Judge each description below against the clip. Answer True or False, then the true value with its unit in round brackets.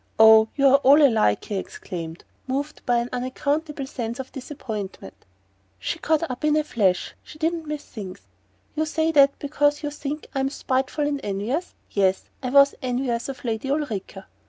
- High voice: True (265 Hz)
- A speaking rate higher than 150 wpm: True (170 wpm)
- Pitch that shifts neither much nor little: True (4.9 semitones)